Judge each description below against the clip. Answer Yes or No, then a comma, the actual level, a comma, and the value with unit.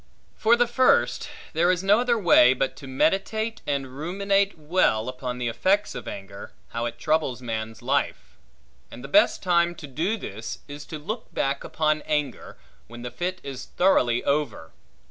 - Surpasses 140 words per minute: Yes, average, 170 wpm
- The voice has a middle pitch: Yes, medium, 150 Hz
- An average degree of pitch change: No, wide, 7.4 semitones